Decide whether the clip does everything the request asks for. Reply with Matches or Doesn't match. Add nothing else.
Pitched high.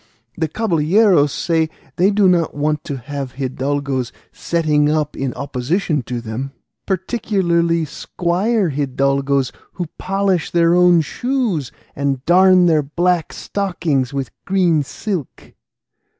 Doesn't match